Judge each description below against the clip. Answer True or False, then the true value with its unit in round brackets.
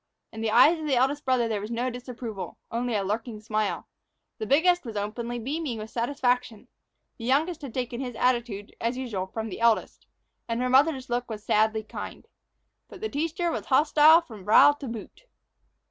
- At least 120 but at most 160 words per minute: False (185 wpm)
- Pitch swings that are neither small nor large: True (3.8 semitones)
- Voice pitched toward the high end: True (240 Hz)